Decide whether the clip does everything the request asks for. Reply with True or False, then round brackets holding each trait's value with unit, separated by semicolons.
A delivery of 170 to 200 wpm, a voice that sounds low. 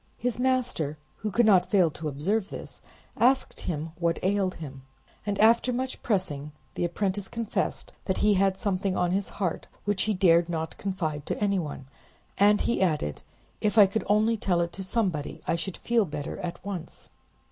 False (180 wpm; 190 Hz)